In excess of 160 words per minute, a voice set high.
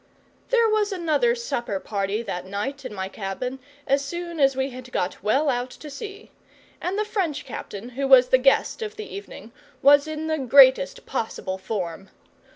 Yes: average, 175 wpm; very high, 275 Hz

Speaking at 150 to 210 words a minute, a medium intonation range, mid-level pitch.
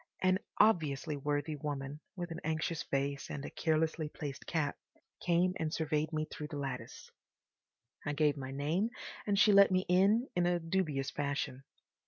Yes: average, 165 wpm; average, 3.5 semitones; medium, 155 Hz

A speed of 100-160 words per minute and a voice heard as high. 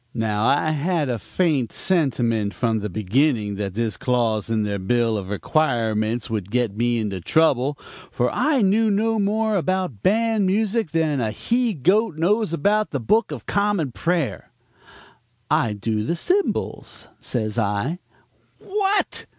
No: average, 150 wpm; low, 135 Hz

